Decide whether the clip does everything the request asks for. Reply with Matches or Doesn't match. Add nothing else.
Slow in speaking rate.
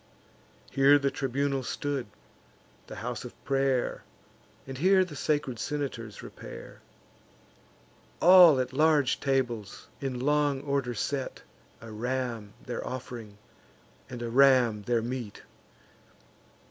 Matches